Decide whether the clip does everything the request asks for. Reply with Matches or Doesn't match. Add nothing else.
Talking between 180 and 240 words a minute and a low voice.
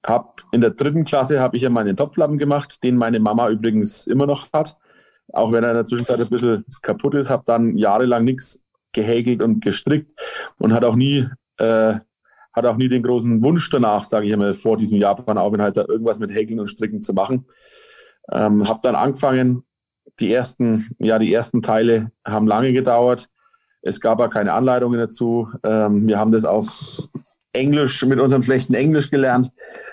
Matches